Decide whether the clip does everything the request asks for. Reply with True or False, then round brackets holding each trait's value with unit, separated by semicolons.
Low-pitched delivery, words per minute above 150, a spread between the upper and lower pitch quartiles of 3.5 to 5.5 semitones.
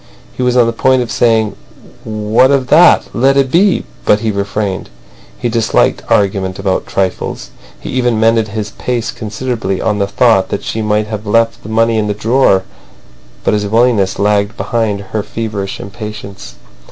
False (110 Hz; 170 wpm; 2.5 semitones)